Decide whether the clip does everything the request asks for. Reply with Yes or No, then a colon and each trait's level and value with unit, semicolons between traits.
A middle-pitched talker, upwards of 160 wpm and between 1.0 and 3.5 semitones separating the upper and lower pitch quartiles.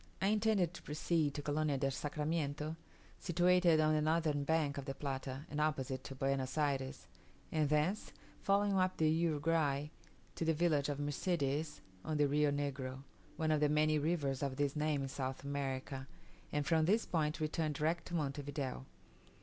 Yes: medium, 150 Hz; average, 175 wpm; narrow, 2.5 semitones